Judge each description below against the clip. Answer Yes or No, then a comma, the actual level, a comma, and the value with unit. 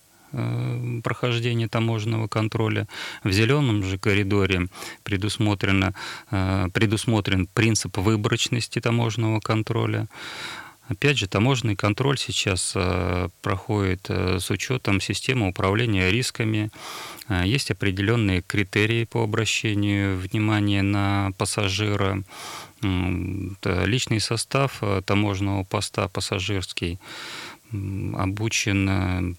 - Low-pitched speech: Yes, low, 105 Hz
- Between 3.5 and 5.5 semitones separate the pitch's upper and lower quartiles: No, average, 2.7 semitones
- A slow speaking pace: Yes, slow, 80 wpm